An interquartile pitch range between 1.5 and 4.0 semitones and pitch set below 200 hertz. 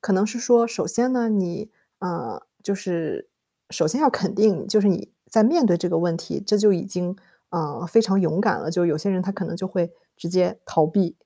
Yes: average, 3.7 semitones; high, 190 Hz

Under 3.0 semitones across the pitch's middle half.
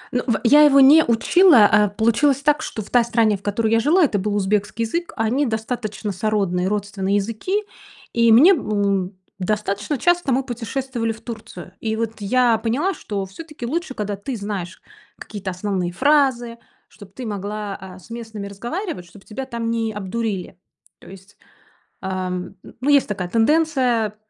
No: average, 4.1 semitones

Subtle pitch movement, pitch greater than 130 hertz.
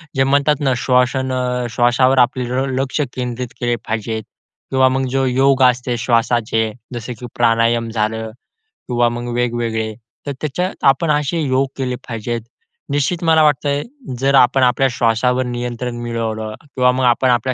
No: narrow, 2.2 semitones; low, 125 Hz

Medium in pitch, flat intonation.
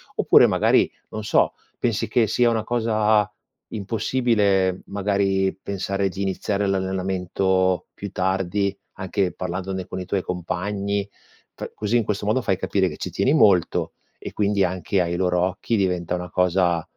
No: very low, 95 Hz; narrow, 1.9 semitones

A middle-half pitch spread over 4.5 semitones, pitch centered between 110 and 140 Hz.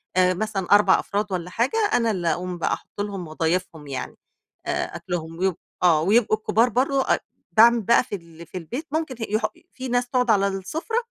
No: average, 5.2 semitones; high, 200 Hz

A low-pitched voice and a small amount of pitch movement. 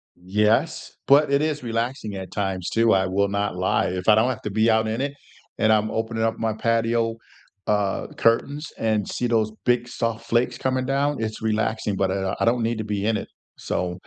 Yes: low, 110 Hz; narrow, 2.3 semitones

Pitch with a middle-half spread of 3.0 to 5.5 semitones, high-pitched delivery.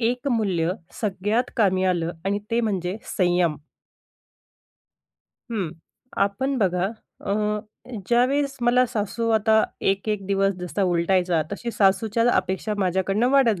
Yes: average, 3.7 semitones; high, 200 Hz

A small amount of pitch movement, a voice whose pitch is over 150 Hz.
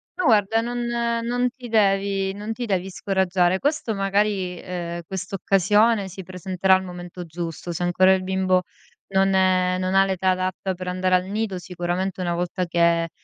Yes: narrow, 1.8 semitones; high, 190 Hz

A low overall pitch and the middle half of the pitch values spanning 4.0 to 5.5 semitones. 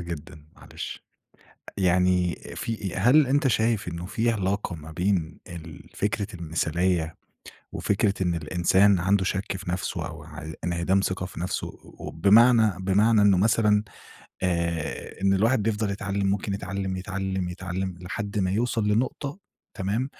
No: very low, 95 Hz; average, 2.9 semitones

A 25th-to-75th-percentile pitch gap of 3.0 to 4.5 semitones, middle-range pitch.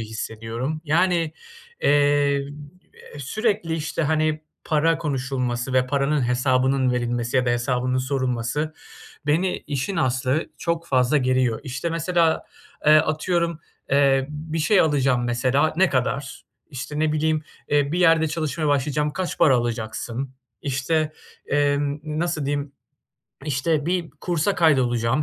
Yes: average, 3.6 semitones; medium, 145 Hz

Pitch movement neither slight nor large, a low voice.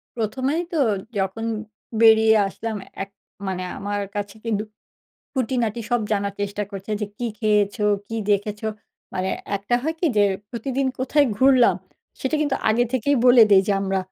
No: average, 3.5 semitones; high, 220 Hz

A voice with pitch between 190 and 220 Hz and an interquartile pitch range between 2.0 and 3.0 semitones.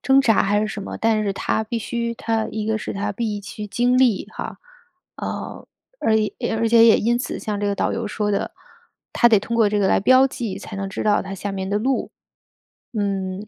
Yes: high, 215 Hz; narrow, 2.4 semitones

